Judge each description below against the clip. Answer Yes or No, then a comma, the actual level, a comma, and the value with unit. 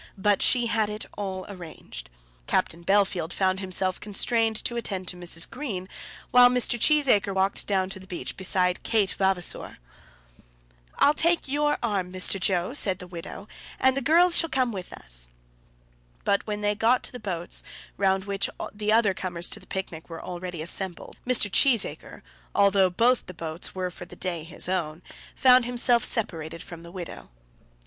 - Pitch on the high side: Yes, high, 195 Hz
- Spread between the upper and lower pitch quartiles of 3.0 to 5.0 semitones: Yes, average, 4.3 semitones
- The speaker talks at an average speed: Yes, average, 170 wpm